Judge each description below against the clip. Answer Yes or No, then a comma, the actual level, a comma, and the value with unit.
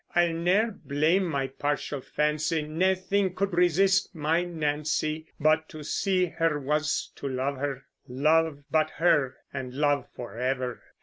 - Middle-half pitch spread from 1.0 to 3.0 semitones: No, average, 3.4 semitones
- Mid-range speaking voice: Yes, medium, 155 Hz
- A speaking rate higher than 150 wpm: No, slow, 135 wpm